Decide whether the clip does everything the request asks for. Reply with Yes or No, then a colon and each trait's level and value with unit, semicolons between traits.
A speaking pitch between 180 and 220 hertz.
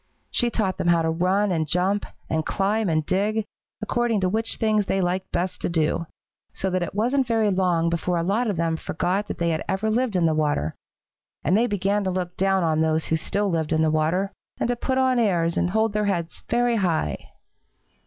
Yes: medium, 185 Hz